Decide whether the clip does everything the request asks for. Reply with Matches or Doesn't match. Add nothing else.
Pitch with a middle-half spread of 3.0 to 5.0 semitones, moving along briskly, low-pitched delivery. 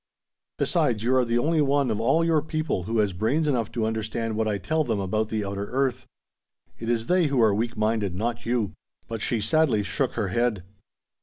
Matches